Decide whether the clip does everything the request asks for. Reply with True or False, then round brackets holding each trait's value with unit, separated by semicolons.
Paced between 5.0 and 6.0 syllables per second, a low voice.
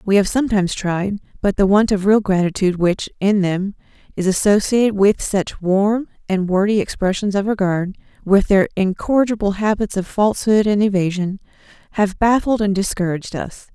False (5.3 syllables/s; 200 Hz)